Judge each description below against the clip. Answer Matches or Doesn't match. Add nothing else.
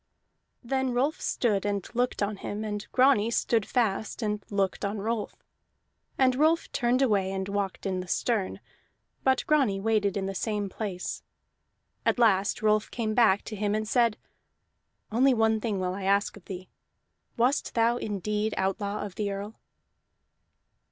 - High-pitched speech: Matches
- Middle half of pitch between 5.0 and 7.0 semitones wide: Doesn't match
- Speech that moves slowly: Doesn't match